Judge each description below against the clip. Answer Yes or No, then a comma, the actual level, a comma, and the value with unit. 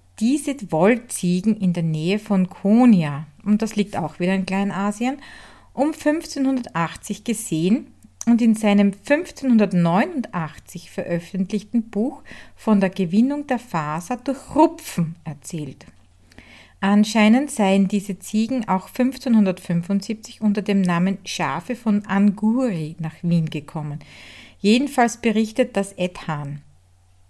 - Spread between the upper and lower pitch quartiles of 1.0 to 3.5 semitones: No, wide, 5.4 semitones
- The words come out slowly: Yes, slow, 110 wpm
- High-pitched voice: Yes, high, 200 Hz